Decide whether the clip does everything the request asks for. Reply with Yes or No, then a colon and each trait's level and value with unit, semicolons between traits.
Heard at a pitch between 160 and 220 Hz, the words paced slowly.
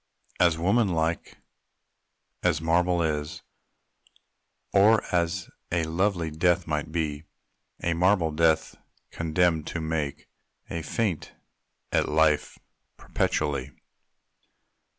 No: very low, 80 Hz; slow, 95 wpm